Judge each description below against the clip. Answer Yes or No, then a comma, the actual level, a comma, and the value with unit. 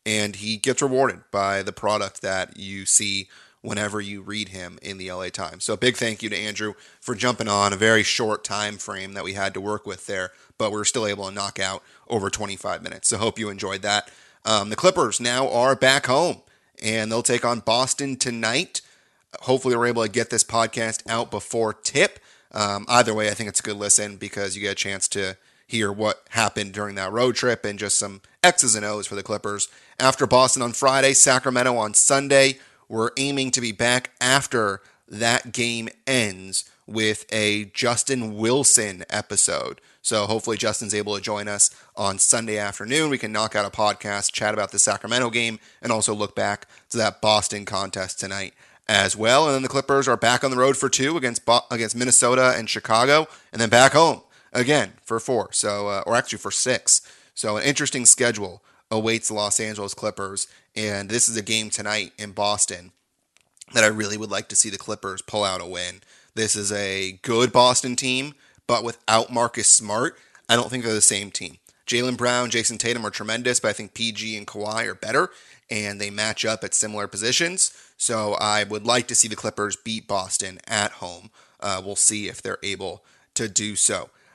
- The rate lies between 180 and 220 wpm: Yes, average, 200 wpm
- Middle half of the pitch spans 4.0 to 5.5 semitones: No, average, 2.8 semitones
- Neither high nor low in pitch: No, low, 110 Hz